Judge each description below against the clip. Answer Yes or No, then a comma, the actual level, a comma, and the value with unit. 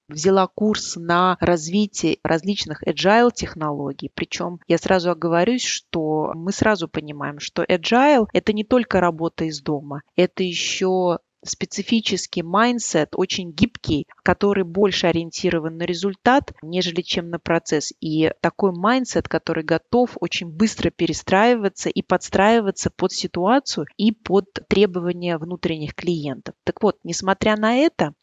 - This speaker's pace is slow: No, average, 130 wpm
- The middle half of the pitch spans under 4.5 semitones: Yes, average, 3.4 semitones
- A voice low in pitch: No, medium, 180 Hz